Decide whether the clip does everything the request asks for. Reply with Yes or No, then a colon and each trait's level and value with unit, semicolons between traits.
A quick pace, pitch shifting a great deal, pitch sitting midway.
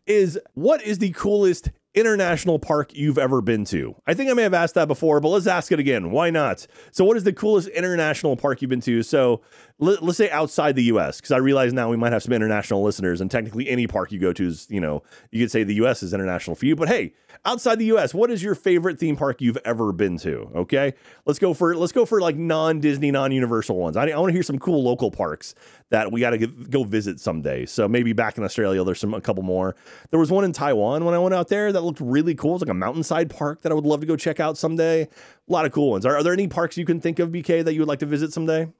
Yes: fast, 270 wpm; wide, 6.6 semitones; medium, 150 Hz